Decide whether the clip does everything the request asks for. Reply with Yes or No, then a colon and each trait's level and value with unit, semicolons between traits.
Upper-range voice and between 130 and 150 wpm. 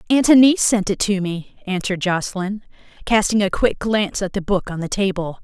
No: high, 200 Hz; average, 200 wpm